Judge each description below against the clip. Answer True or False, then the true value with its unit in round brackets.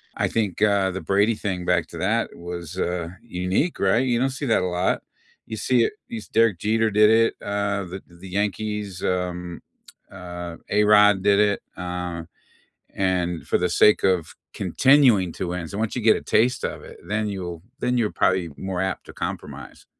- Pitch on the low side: True (100 Hz)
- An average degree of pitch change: True (3.2 semitones)